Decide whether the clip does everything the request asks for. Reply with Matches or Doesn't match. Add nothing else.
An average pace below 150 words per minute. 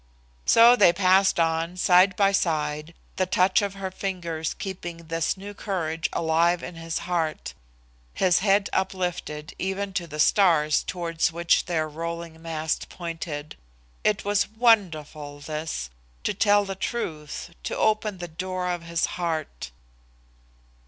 Matches